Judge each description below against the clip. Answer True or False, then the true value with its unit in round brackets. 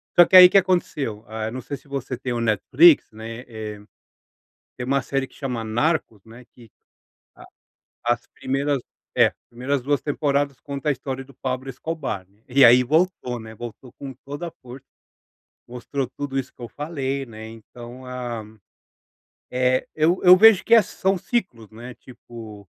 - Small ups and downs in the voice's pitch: False (3.4 semitones)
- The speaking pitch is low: True (130 Hz)